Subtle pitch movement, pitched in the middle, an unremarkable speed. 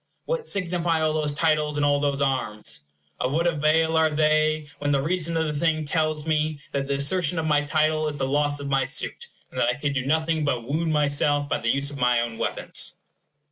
No: narrow, 2.0 semitones; medium, 150 Hz; fast, 220 wpm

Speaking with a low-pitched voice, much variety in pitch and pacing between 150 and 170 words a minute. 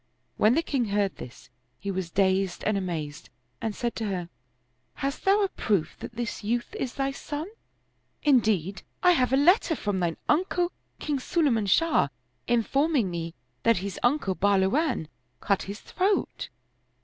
No: high, 225 Hz; wide, 7.0 semitones; average, 160 wpm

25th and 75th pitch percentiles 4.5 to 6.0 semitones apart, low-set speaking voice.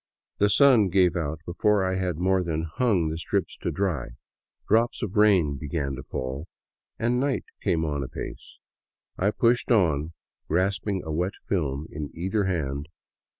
Yes: average, 4.8 semitones; very low, 90 Hz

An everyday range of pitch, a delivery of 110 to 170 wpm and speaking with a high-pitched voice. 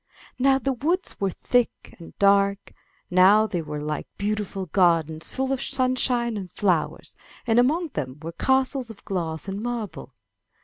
No: wide, 6.5 semitones; average, 150 wpm; high, 200 Hz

